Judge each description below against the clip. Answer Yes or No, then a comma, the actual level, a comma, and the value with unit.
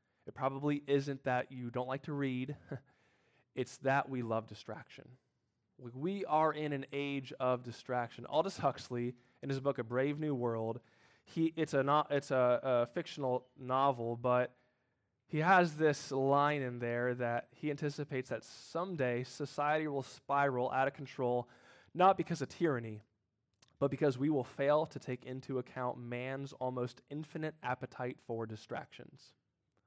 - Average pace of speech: Yes, average, 155 wpm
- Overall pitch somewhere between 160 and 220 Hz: No, low, 130 Hz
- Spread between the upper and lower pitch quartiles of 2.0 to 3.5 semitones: Yes, average, 2.8 semitones